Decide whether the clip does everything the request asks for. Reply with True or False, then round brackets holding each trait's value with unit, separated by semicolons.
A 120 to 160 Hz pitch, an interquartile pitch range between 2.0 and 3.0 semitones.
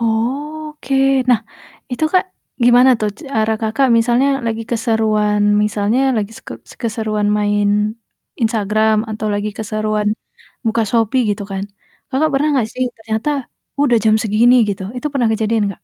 False (220 Hz; 2.6 semitones)